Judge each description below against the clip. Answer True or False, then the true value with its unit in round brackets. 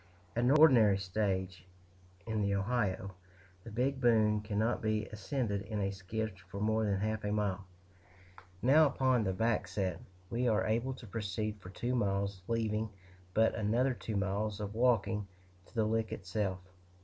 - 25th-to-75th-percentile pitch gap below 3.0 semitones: True (2.6 semitones)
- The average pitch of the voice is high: False (110 Hz)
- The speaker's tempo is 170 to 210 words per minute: False (160 wpm)